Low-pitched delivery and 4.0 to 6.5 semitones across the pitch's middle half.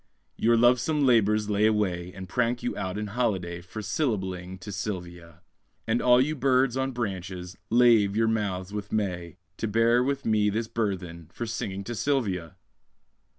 Yes: low, 105 Hz; average, 4.4 semitones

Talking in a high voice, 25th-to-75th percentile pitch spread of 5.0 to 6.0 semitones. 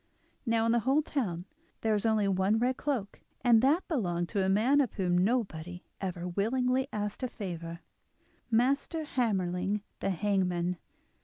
Yes: high, 210 Hz; wide, 5.5 semitones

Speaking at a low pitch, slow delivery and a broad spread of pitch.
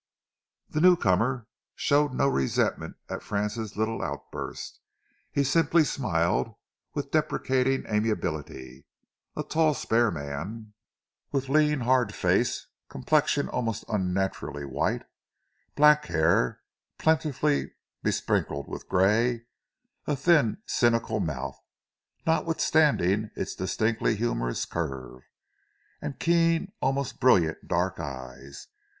Yes: low, 115 Hz; slow, 100 wpm; wide, 8.5 semitones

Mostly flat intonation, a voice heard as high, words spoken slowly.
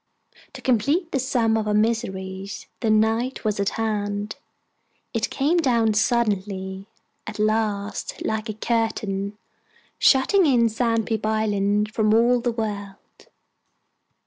Yes: narrow, 2.3 semitones; high, 220 Hz; slow, 120 wpm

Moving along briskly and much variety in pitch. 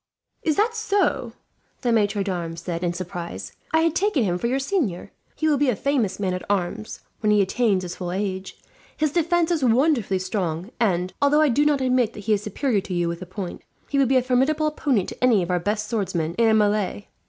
Yes: fast, 225 wpm; wide, 7.1 semitones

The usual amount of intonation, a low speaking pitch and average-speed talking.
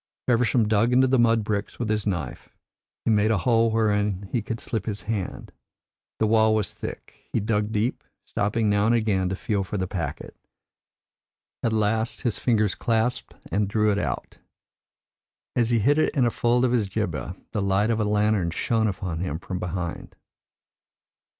No: narrow, 2.3 semitones; low, 110 Hz; average, 180 wpm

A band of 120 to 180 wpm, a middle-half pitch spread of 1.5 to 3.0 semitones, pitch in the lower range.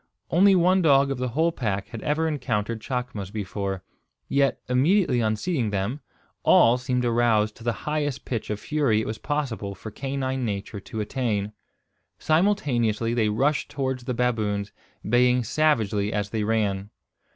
No: average, 155 wpm; average, 4.6 semitones; low, 120 Hz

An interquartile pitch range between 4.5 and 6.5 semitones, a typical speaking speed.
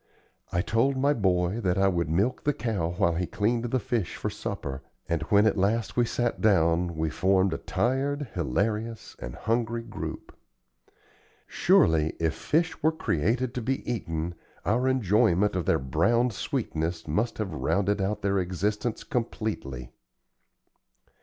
Yes: wide, 5.4 semitones; average, 150 wpm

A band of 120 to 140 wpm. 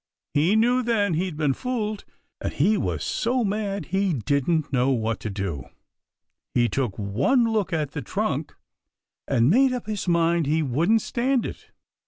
No: average, 165 wpm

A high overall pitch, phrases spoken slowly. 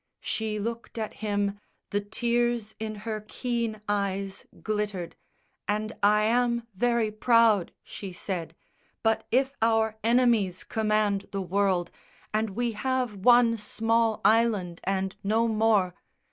Yes: high, 215 Hz; slow, 125 wpm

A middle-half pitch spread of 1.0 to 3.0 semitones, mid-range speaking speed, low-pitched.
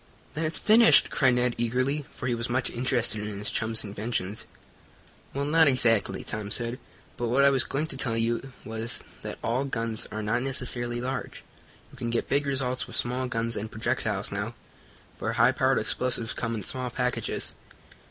Yes: narrow, 2.5 semitones; average, 180 wpm; low, 120 Hz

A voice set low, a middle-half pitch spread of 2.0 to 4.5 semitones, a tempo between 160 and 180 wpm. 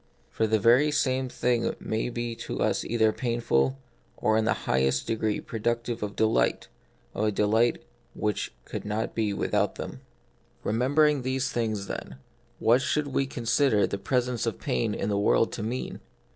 Yes: low, 115 Hz; average, 2.8 semitones; average, 165 wpm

